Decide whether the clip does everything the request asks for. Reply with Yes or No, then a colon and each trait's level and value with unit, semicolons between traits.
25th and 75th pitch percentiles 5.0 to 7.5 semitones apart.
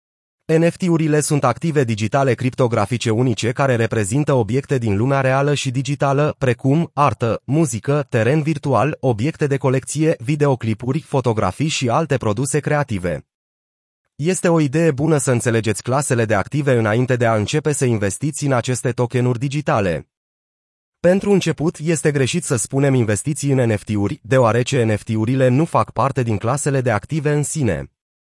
No: average, 4.2 semitones